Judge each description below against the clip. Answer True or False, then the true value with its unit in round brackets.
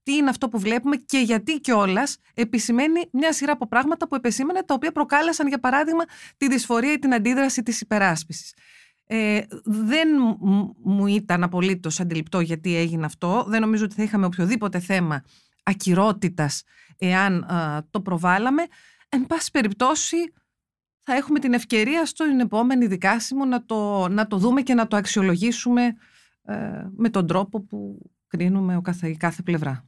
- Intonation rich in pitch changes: True (6.1 semitones)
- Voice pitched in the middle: False (220 Hz)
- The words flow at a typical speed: True (155 wpm)